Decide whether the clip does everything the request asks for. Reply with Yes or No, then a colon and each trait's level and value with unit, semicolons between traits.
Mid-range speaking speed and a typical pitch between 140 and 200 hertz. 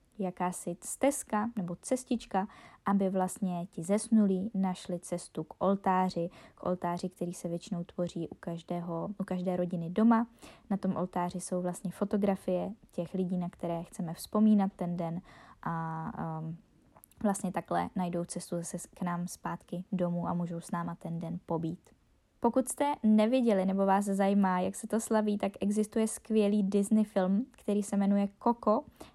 Yes: average, 155 wpm; medium, 185 Hz